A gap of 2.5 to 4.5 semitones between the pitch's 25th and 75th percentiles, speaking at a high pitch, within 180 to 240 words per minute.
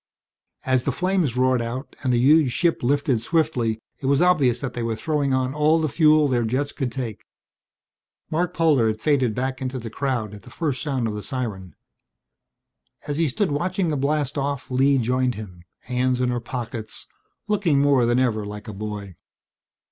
No: average, 3.8 semitones; low, 130 Hz; average, 185 wpm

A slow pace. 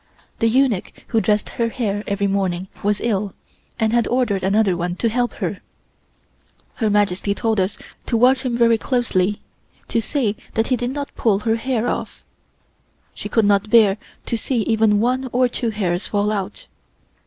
No: average, 175 wpm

